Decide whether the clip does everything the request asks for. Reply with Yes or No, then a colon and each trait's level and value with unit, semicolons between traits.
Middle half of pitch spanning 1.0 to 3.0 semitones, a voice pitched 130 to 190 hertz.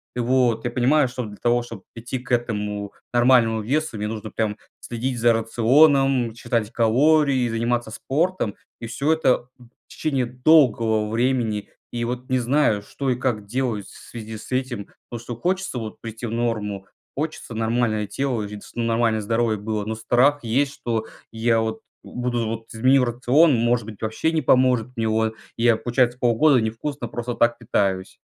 No: narrow, 2.5 semitones; low, 120 Hz